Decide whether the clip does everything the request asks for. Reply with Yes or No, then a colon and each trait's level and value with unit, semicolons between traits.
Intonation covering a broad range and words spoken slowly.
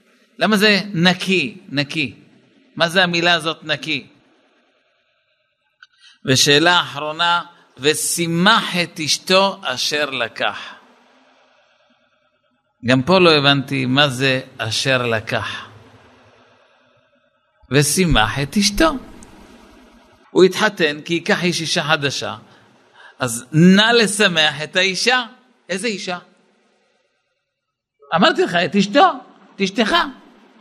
Yes: wide, 6.0 semitones; slow, 90 wpm